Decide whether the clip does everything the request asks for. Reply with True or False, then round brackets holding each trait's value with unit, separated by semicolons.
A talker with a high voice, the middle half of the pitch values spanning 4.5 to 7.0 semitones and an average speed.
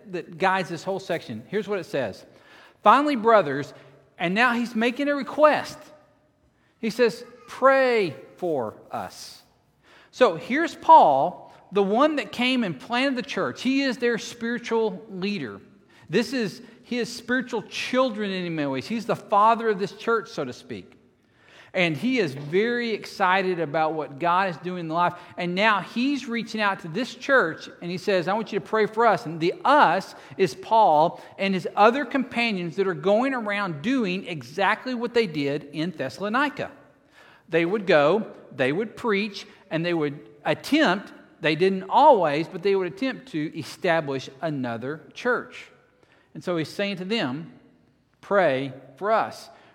True (205 Hz; 5.4 semitones; 165 wpm)